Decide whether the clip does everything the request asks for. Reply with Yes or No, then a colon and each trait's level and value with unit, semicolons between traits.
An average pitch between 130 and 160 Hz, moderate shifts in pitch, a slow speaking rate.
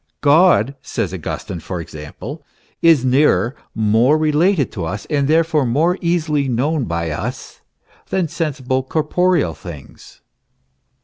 No: medium, 140 Hz; wide, 6.2 semitones; slow, 120 wpm